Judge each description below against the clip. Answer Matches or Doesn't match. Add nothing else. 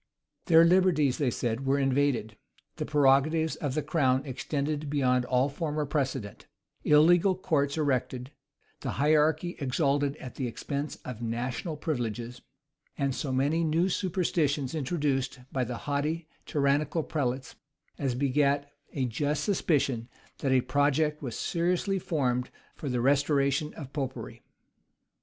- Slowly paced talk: Matches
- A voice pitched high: Doesn't match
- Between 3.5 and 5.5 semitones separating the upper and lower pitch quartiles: Doesn't match